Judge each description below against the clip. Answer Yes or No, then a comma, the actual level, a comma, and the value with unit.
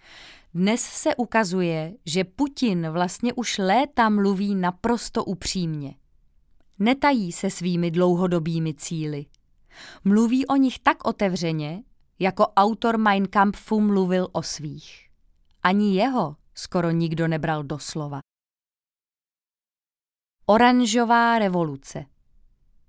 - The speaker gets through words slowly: Yes, slow, 95 wpm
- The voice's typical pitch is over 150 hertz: Yes, medium, 185 Hz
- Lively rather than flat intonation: Yes, wide, 5.9 semitones